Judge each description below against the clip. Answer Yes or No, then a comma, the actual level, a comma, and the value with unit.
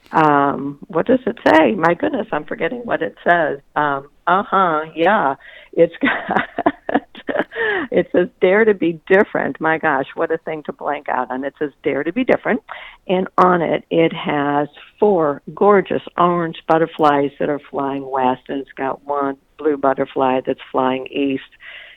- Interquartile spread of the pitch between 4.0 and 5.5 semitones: Yes, average, 4.8 semitones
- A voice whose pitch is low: No, medium, 155 Hz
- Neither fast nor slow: Yes, average, 165 wpm